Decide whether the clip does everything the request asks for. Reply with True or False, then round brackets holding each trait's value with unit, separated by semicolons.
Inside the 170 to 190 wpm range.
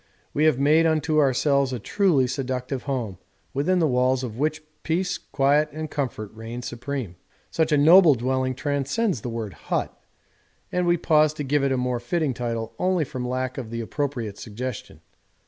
True (175 wpm)